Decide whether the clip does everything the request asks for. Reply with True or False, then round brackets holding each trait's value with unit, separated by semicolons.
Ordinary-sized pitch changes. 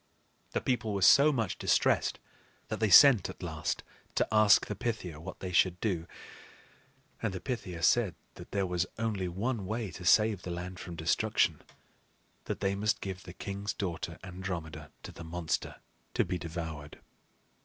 True (3.8 semitones)